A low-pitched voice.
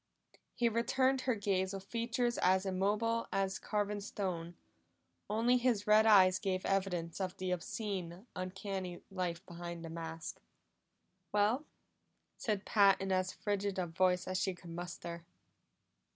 No: high, 195 Hz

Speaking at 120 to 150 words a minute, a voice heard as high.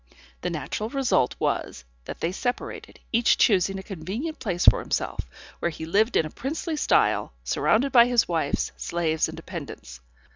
No: average, 160 wpm; high, 195 Hz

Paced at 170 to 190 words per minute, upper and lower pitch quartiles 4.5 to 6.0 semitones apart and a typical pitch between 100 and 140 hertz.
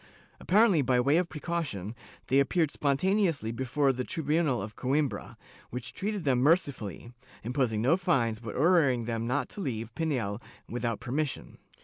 No: average, 150 wpm; average, 5.3 semitones; low, 135 Hz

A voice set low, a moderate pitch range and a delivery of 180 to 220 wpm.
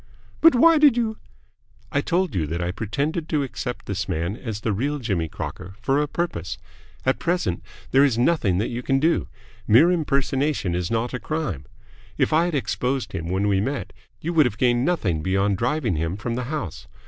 No: low, 125 Hz; wide, 7.9 semitones; average, 200 wpm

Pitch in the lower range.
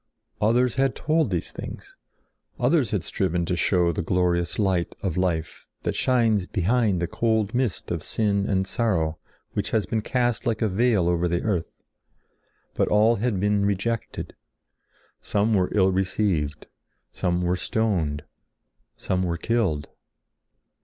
Yes: low, 100 Hz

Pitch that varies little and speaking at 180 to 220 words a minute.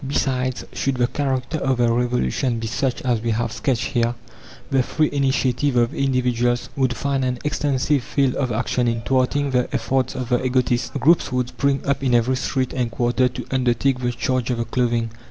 Yes: narrow, 1.8 semitones; average, 190 wpm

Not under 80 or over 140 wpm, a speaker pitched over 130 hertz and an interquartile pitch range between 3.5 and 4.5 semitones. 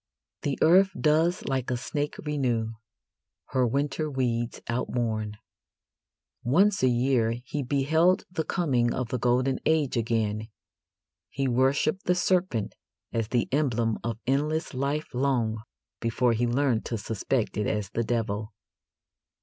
No: slow, 135 wpm; low, 125 Hz; average, 4.1 semitones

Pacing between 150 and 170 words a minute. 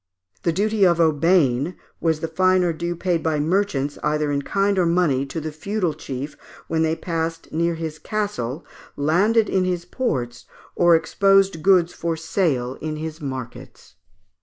Yes: average, 160 wpm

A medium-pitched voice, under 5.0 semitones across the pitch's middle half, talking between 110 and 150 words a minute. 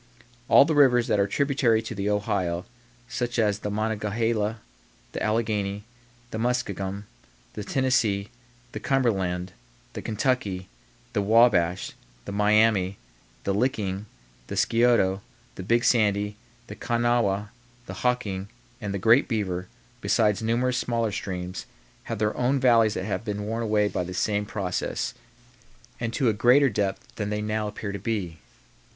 No: low, 105 Hz; average, 2.9 semitones; average, 145 wpm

